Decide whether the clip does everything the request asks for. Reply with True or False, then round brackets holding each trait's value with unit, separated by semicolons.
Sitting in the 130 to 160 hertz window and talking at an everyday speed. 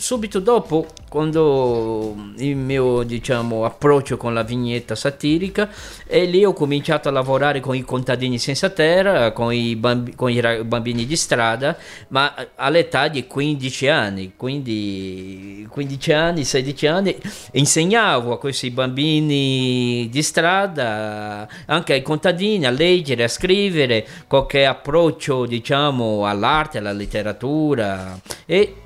True (135 Hz; 125 wpm)